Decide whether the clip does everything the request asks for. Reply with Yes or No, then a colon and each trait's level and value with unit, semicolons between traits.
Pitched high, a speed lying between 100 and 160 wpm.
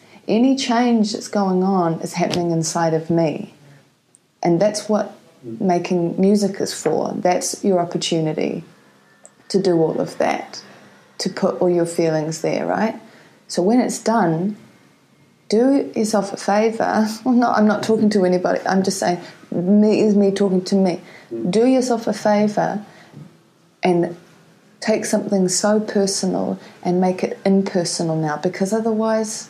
Yes: high, 195 Hz; average, 145 wpm